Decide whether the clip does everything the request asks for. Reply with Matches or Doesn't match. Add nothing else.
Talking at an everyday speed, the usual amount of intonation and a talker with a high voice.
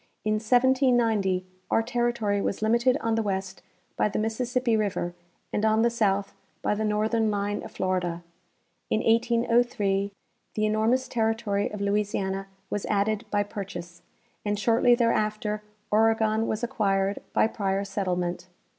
Doesn't match